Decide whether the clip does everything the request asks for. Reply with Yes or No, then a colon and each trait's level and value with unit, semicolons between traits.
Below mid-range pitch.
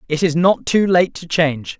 No: medium, 165 Hz